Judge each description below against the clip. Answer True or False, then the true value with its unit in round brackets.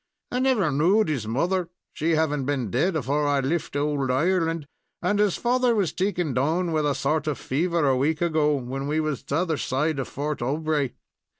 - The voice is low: False (155 Hz)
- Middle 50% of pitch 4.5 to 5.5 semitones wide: False (3.7 semitones)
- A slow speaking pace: False (190 wpm)